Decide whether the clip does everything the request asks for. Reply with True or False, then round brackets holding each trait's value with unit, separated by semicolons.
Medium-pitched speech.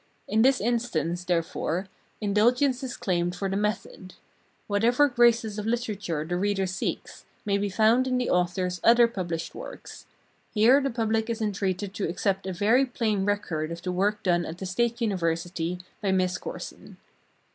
False (205 Hz)